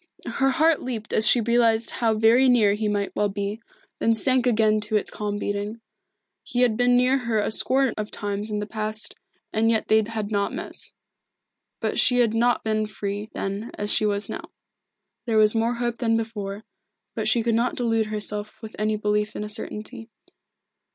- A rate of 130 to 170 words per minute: No, average, 195 wpm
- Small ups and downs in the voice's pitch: Yes, narrow, 1.9 semitones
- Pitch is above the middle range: Yes, high, 220 Hz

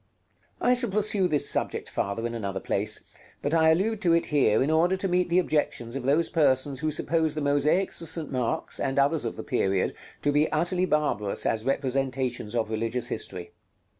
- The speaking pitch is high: No, medium, 145 Hz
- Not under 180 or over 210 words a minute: Yes, average, 200 wpm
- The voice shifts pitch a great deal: Yes, wide, 5.7 semitones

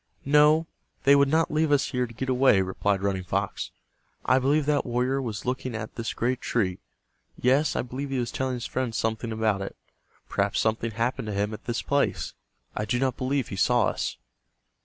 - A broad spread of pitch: No, average, 3.5 semitones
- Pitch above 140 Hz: No, low, 125 Hz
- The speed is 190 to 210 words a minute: Yes, average, 200 wpm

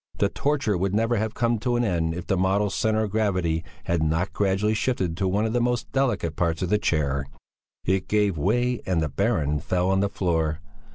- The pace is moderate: No, fast, 215 wpm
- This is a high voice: No, very low, 95 Hz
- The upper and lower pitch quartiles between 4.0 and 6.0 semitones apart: Yes, average, 4.7 semitones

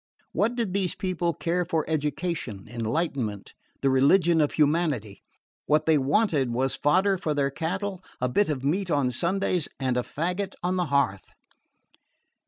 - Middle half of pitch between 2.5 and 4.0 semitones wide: No, average, 5.2 semitones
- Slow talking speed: No, average, 155 wpm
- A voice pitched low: No, medium, 155 Hz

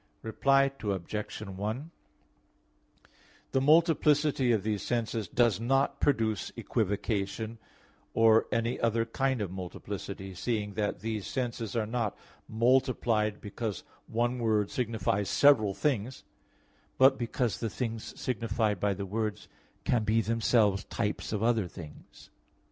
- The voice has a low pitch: Yes, low, 110 Hz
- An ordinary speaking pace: No, slow, 120 wpm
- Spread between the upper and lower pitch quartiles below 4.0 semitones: Yes, average, 2.8 semitones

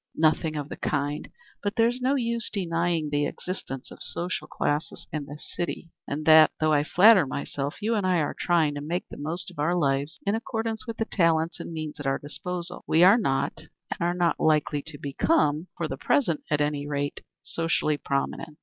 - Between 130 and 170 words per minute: No, average, 200 wpm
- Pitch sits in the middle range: Yes, medium, 160 Hz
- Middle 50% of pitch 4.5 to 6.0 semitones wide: No, average, 3.7 semitones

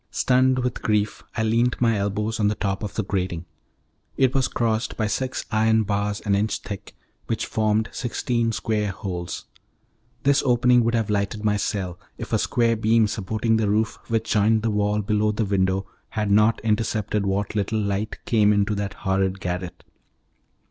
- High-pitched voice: No, low, 105 Hz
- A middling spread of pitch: No, narrow, 1.9 semitones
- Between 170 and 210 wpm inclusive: Yes, average, 175 wpm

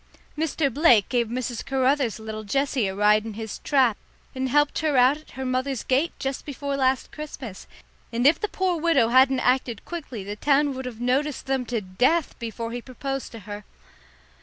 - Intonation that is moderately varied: Yes, average, 3.5 semitones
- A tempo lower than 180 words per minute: No, average, 185 wpm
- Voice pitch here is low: No, very high, 260 Hz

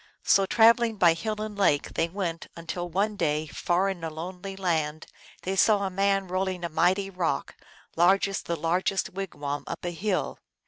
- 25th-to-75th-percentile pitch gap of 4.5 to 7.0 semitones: No, average, 2.8 semitones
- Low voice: No, medium, 185 Hz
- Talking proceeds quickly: No, average, 180 wpm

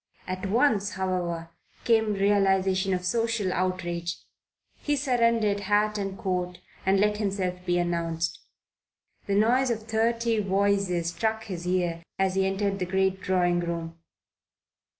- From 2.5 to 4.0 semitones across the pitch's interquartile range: Yes, average, 2.8 semitones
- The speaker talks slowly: Yes, slow, 130 wpm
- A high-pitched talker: Yes, high, 195 Hz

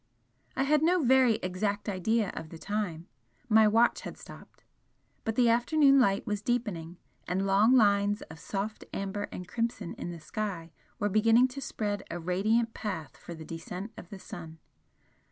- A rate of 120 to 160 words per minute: No, average, 170 wpm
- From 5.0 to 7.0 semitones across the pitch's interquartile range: No, average, 4.2 semitones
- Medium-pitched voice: No, high, 205 Hz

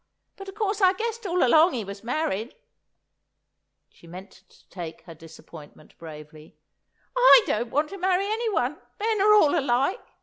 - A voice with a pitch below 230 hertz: No, very high, 300 Hz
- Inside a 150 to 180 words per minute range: Yes, average, 160 wpm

